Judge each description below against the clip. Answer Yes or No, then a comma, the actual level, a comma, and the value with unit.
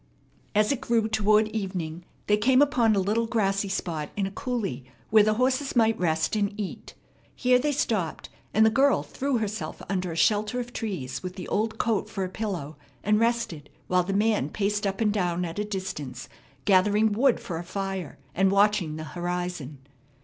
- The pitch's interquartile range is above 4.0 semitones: No, average, 3.6 semitones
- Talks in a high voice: Yes, high, 205 Hz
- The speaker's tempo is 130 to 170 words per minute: No, average, 185 wpm